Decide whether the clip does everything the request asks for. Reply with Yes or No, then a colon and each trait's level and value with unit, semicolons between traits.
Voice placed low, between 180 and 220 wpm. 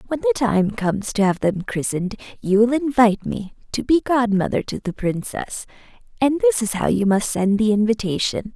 No: high, 225 Hz; average, 190 wpm